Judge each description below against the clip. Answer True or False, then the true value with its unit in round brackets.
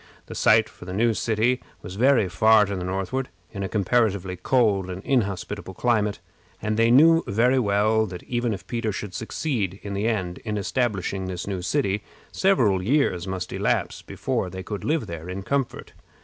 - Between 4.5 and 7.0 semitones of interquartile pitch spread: False (3.9 semitones)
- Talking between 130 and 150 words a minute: False (180 wpm)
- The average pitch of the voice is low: True (105 Hz)